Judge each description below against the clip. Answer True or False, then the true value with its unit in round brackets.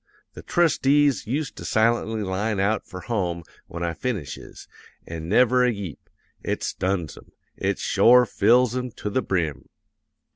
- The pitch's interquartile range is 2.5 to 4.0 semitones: False (5.3 semitones)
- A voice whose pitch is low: True (110 Hz)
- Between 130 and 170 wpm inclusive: True (150 wpm)